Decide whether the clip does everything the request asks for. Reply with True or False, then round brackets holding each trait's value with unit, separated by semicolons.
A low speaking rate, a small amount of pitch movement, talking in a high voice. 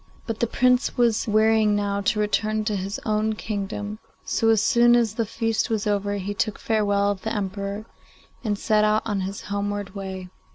False (190 wpm; 1.5 semitones; 210 Hz)